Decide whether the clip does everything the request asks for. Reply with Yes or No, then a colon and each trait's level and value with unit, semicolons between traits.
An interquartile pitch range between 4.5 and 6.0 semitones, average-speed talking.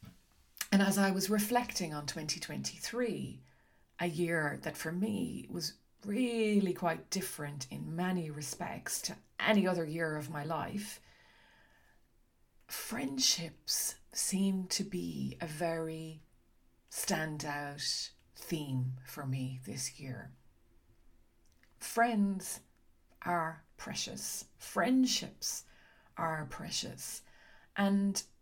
No: wide, 5.5 semitones; slow, 95 wpm